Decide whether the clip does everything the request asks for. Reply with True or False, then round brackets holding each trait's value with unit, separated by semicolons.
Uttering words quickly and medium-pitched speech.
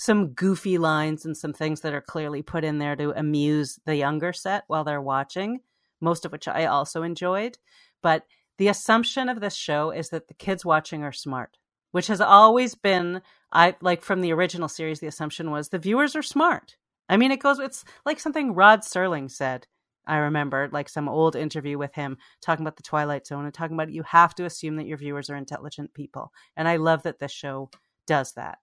True (210 wpm; 160 Hz)